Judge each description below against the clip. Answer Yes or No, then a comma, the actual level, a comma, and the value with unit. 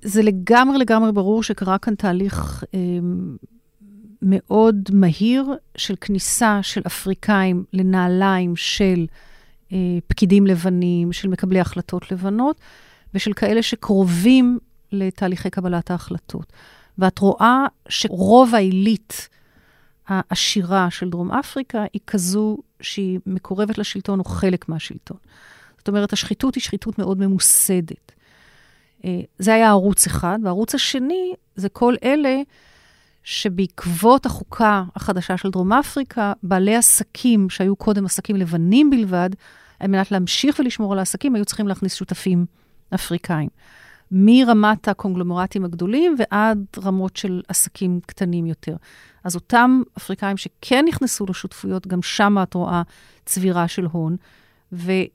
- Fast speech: No, average, 120 wpm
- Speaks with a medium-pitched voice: No, high, 195 Hz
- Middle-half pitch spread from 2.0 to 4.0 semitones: Yes, average, 3.0 semitones